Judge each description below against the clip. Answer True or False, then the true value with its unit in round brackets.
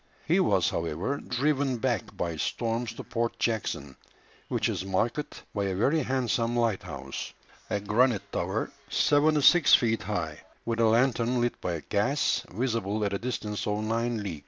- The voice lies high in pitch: False (115 Hz)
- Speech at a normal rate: True (160 wpm)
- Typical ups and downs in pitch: True (3.7 semitones)